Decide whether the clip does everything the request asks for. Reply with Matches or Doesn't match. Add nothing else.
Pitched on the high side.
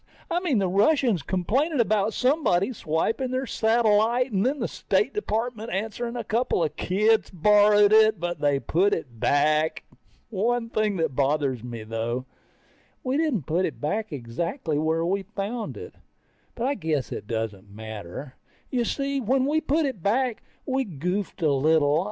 Matches